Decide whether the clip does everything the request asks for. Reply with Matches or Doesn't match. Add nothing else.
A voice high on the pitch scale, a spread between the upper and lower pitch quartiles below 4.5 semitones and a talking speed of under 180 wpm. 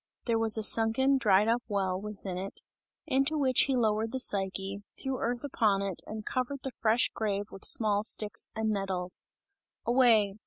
Matches